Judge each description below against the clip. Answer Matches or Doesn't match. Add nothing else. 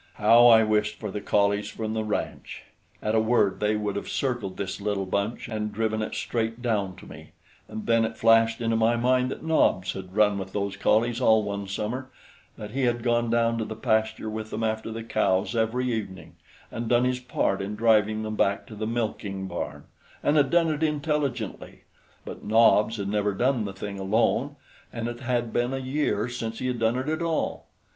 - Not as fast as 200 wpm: Doesn't match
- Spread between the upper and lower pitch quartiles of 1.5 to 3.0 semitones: Matches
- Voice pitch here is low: Matches